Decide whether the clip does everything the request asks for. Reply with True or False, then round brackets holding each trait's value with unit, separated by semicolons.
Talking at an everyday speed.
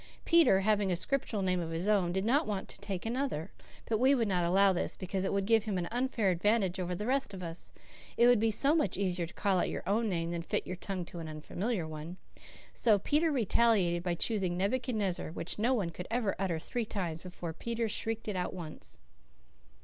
False (220 wpm)